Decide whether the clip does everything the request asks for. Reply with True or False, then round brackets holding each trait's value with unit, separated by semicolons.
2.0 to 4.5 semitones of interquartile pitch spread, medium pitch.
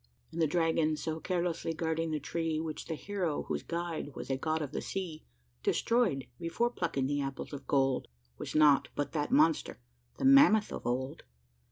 True (2.7 semitones; 160 Hz)